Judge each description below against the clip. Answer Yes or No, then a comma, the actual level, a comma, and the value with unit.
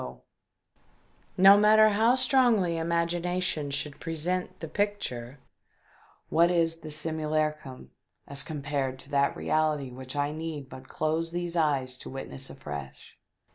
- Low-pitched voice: No, medium, 155 Hz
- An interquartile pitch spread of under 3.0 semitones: No, average, 4.0 semitones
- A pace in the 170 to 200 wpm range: No, slow, 135 wpm